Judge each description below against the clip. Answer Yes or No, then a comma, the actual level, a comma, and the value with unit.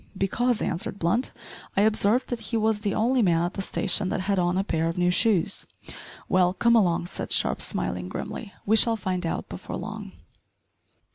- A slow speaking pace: No, average, 190 wpm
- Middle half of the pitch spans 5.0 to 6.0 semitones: No, average, 4.0 semitones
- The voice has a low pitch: No, high, 195 Hz